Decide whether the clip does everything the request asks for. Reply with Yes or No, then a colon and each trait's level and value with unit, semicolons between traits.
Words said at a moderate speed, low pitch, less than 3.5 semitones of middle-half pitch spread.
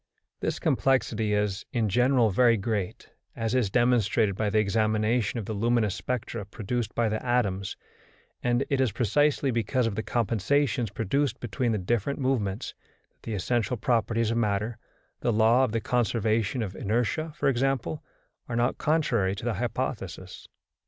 Yes: average, 160 wpm; low, 115 Hz; average, 2.8 semitones